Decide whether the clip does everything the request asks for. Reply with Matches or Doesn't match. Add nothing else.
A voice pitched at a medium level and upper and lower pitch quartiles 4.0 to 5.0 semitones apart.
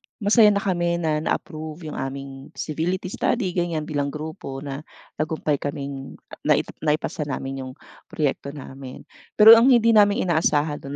Matches